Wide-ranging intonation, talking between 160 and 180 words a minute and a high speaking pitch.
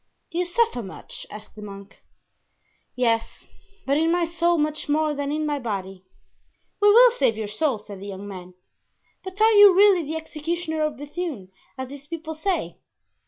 Yes: wide, 8.0 semitones; average, 175 wpm; very high, 300 Hz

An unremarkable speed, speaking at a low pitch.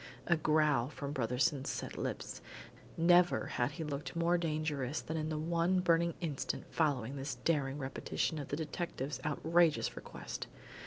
No: average, 150 wpm; medium, 155 Hz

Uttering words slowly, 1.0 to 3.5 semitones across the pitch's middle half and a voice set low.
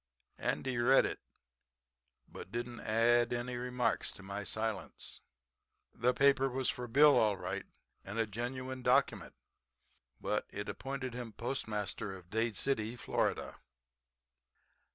Yes: slow, 125 wpm; average, 2.9 semitones; low, 120 Hz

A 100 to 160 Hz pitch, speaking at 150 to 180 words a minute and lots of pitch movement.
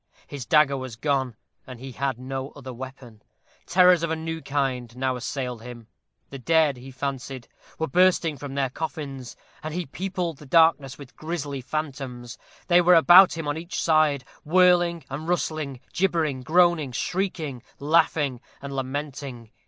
No: medium, 140 Hz; average, 160 wpm; average, 3.8 semitones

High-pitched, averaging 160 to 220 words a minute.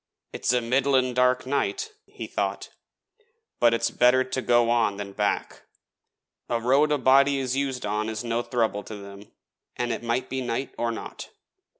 No: low, 120 Hz; average, 170 wpm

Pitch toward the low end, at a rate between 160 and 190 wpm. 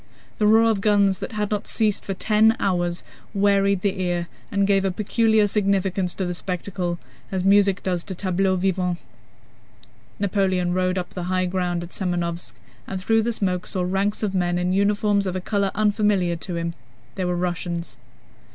No: high, 190 Hz; average, 180 wpm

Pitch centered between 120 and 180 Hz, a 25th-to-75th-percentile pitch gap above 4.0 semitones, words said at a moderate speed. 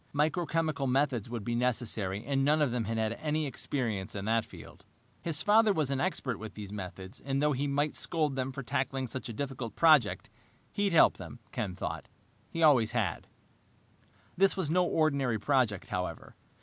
Yes: low, 135 Hz; average, 5.1 semitones; average, 180 wpm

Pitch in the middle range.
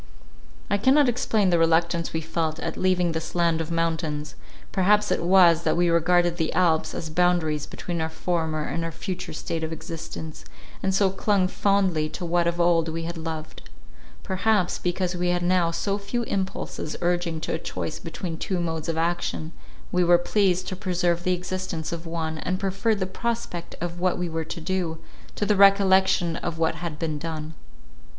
Yes: medium, 175 Hz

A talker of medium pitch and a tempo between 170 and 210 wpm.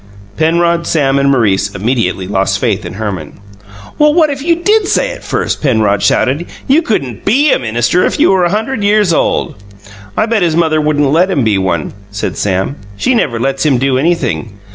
Yes: medium, 145 Hz; average, 190 wpm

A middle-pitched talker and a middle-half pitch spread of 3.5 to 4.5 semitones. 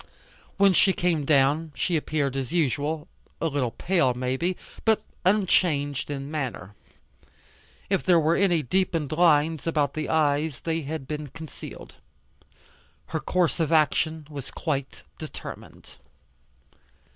No: medium, 155 Hz; average, 3.0 semitones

